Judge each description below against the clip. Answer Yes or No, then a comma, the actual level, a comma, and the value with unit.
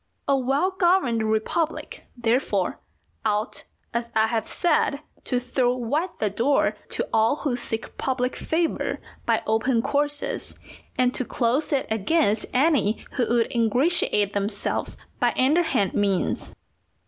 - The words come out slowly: Yes, slow, 130 wpm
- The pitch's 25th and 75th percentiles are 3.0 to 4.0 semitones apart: No, average, 4.6 semitones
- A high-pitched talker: Yes, very high, 250 Hz